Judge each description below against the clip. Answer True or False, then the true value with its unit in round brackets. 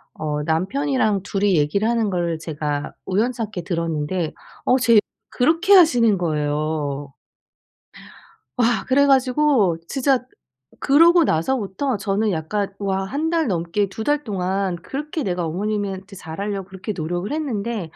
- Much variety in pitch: True (6.8 semitones)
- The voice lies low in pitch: False (200 Hz)